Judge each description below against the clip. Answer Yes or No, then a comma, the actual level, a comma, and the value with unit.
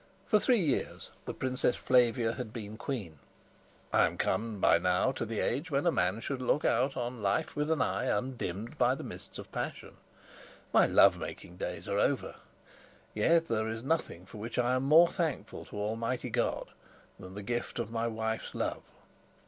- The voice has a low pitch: Yes, low, 120 Hz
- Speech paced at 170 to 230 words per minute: Yes, average, 185 wpm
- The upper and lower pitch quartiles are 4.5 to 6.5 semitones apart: No, average, 3.7 semitones